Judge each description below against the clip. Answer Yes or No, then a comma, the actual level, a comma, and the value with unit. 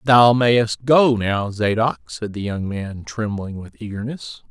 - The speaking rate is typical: Yes, average, 160 wpm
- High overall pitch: No, low, 110 Hz